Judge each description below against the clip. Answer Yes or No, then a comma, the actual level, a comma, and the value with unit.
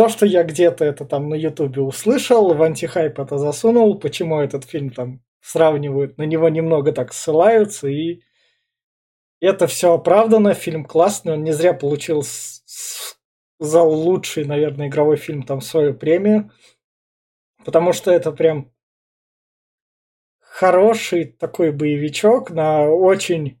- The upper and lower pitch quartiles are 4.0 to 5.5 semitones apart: No, average, 3.4 semitones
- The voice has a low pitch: No, medium, 160 Hz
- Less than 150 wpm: Yes, average, 130 wpm